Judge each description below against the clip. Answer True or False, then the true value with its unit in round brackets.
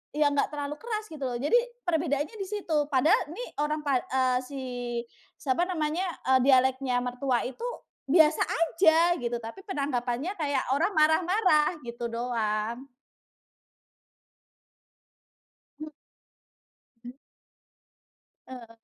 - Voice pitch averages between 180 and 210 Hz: False (290 Hz)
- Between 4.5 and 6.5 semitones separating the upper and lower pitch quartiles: True (4.8 semitones)